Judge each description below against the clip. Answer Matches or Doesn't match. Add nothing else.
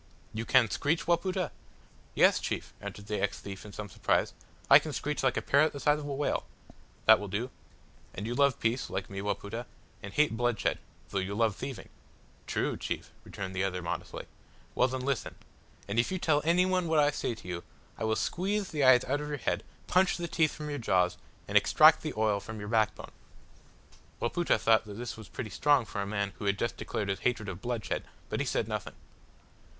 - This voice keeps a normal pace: Doesn't match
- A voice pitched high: Doesn't match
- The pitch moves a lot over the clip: Matches